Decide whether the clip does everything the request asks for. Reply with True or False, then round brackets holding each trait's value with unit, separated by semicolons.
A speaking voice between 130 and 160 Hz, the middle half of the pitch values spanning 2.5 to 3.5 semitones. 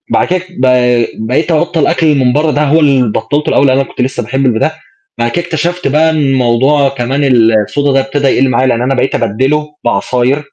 True (135 Hz; 3.1 semitones)